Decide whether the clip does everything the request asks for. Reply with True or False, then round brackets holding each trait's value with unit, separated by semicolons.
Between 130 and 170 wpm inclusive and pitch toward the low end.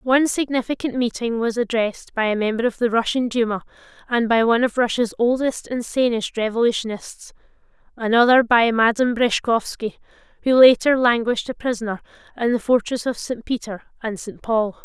False (160 wpm; 235 Hz)